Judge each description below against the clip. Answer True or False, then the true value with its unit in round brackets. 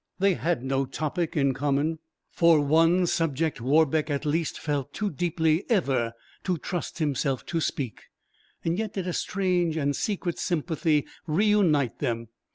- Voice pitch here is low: False (160 Hz)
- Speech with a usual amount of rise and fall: True (3.7 semitones)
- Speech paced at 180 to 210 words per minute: False (150 wpm)